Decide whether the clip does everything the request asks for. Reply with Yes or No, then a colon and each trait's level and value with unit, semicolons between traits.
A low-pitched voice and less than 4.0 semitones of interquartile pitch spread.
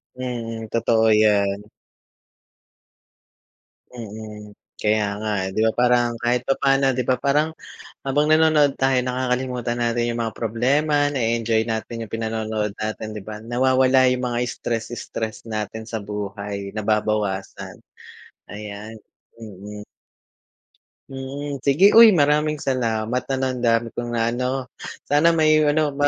Yes: low, 120 Hz; average, 3.5 semitones